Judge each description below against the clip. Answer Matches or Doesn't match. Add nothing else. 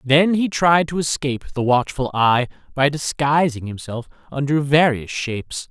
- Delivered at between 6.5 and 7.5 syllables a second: Doesn't match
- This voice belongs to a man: Matches